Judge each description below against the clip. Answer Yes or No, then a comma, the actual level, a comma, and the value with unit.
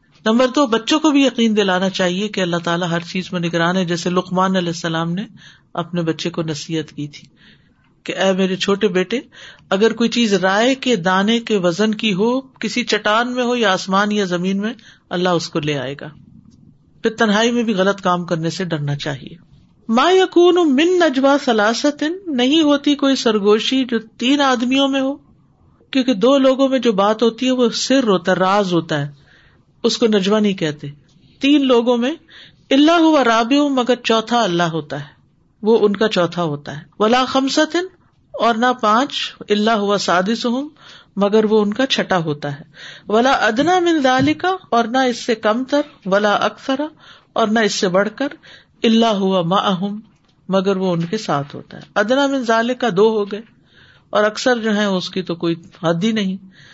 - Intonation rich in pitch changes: Yes, wide, 5.7 semitones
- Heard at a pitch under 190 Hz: No, high, 215 Hz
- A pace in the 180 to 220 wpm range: Yes, average, 185 wpm